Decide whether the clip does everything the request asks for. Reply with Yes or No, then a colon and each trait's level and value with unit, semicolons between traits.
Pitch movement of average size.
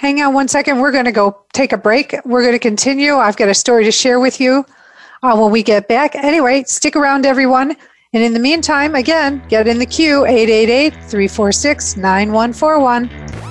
Yes: average, 3.9 semitones